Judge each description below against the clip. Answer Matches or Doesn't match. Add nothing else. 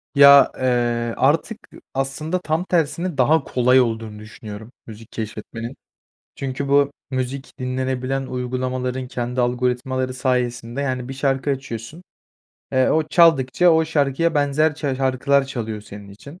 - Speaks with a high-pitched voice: Doesn't match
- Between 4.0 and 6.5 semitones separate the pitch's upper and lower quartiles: Doesn't match